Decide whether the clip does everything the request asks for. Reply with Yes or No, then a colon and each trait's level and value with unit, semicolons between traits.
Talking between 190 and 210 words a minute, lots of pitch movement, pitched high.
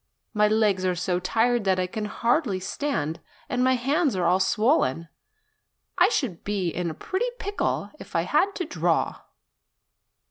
No: average, 165 wpm; wide, 6.1 semitones; high, 210 Hz